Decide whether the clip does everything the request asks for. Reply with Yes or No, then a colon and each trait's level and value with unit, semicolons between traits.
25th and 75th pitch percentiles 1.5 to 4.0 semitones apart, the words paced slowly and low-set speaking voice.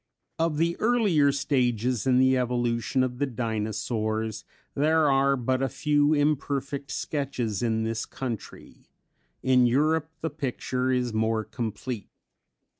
Yes: average, 3.7 semitones; slow, 125 wpm; low, 130 Hz